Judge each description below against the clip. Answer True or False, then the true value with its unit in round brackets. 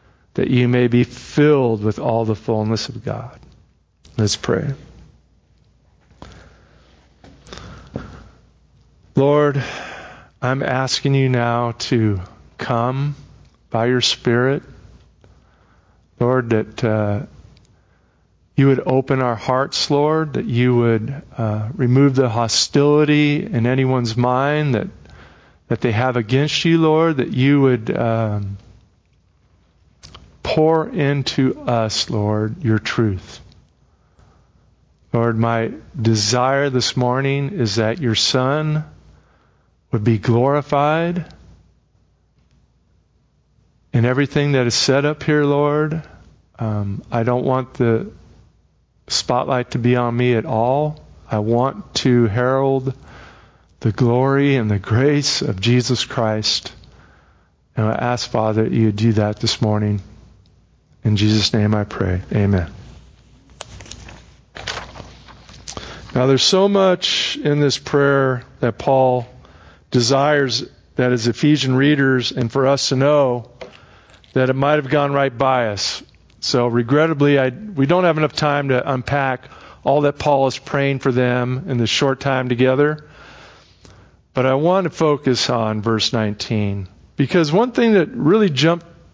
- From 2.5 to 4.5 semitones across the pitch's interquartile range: True (4.0 semitones)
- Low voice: True (125 Hz)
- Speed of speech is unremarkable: False (125 wpm)